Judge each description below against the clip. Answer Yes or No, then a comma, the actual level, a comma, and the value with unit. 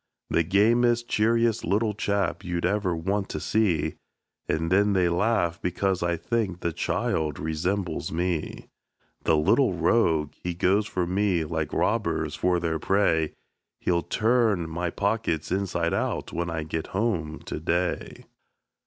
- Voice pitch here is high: No, very low, 90 Hz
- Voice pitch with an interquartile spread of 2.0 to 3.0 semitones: No, average, 3.8 semitones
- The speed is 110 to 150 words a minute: Yes, average, 145 wpm